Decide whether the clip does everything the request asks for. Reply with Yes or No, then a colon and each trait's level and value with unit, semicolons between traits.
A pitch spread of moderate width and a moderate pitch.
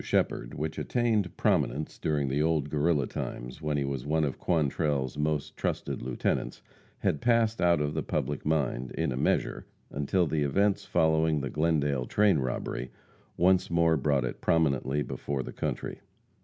No: average, 3.0 semitones; very low, 75 Hz